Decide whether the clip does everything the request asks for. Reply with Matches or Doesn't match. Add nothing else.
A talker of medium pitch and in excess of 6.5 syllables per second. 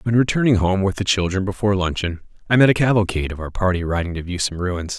Doesn't match